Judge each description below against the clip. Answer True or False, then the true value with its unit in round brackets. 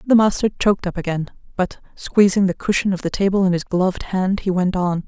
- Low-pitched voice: False (190 Hz)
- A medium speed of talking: False (225 wpm)